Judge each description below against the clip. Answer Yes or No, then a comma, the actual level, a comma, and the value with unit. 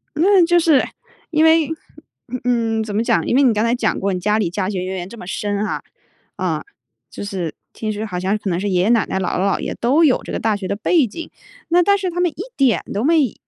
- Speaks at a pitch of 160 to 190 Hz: No, high, 220 Hz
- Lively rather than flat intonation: Yes, wide, 7.5 semitones